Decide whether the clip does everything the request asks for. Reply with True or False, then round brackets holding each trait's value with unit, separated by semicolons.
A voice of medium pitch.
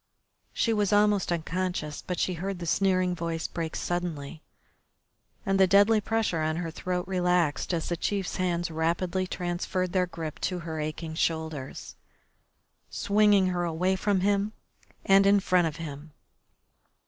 True (180 Hz)